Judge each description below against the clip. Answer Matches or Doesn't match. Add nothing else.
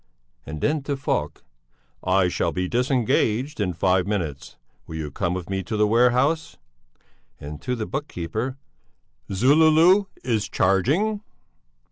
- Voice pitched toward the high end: Doesn't match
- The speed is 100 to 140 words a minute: Matches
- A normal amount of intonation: Doesn't match